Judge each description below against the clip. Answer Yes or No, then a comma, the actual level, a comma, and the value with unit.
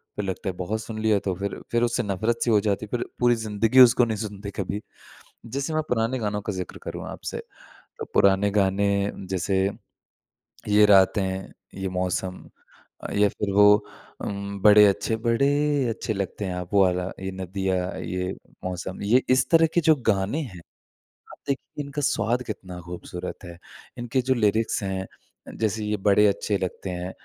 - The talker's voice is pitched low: Yes, low, 105 Hz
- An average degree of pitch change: Yes, average, 3.1 semitones